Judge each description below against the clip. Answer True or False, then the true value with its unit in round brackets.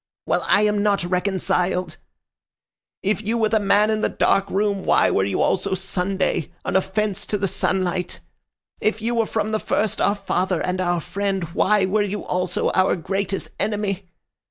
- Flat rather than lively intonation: True (2.2 semitones)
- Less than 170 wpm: False (175 wpm)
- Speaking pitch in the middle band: False (195 Hz)